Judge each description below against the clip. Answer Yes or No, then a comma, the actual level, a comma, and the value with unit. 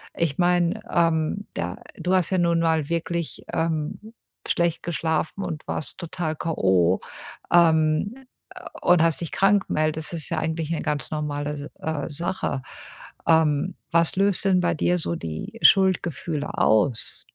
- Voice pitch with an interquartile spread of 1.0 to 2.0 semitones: No, narrow, 2.6 semitones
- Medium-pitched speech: Yes, medium, 165 Hz